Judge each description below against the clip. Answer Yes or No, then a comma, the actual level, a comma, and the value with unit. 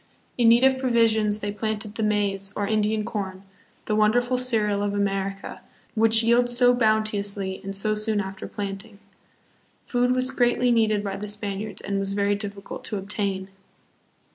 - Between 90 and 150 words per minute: No, average, 160 wpm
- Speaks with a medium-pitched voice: No, high, 210 Hz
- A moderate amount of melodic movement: No, narrow, 2.3 semitones